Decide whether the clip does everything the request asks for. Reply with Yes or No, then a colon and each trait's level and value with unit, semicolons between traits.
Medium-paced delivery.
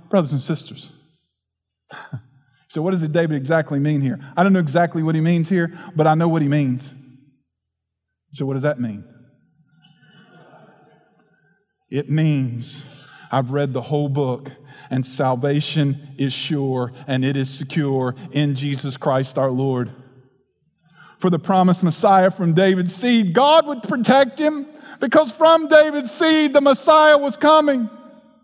Yes: average, 145 wpm